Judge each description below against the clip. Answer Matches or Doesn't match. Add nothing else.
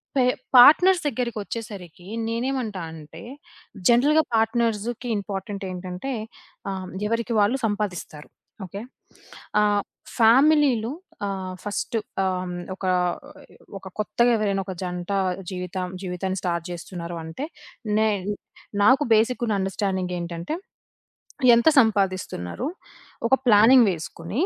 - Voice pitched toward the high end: Matches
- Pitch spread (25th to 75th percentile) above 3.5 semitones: Matches